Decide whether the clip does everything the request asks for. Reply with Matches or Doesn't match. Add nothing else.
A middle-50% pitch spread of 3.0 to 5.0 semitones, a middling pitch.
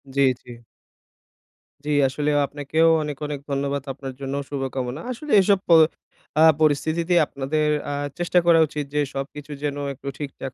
Doesn't match